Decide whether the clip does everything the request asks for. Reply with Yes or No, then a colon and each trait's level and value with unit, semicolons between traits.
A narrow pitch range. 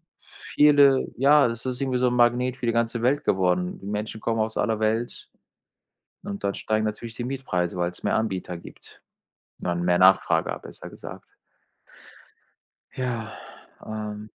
No: average, 3.9 semitones